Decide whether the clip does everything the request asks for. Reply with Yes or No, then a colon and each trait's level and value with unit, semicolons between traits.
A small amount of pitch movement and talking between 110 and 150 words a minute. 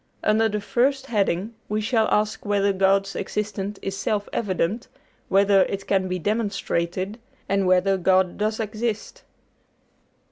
Yes: narrow, 2.0 semitones; slow, 135 wpm